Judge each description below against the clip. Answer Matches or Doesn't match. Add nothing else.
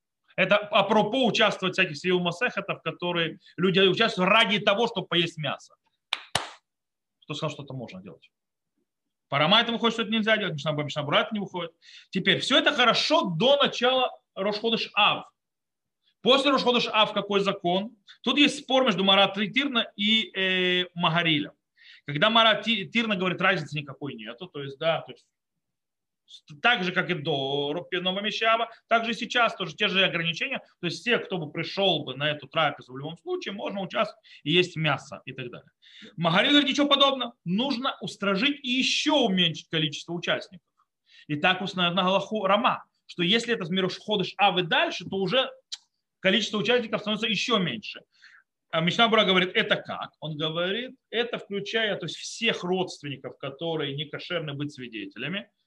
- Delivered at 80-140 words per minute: Doesn't match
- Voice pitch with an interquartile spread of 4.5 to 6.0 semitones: Matches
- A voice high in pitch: Matches